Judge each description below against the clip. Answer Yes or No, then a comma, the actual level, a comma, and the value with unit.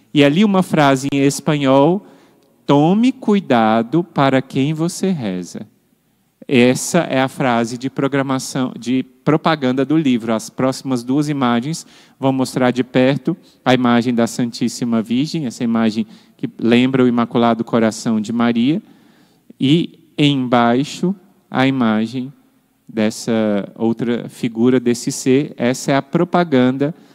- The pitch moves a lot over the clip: No, average, 4.6 semitones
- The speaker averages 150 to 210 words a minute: No, average, 125 wpm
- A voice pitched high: No, low, 130 Hz